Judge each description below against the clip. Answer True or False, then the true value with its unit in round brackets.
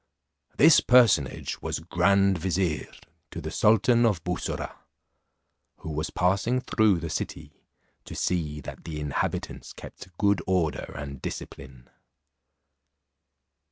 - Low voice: True (90 Hz)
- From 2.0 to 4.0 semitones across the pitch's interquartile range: False (4.7 semitones)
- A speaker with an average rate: False (115 wpm)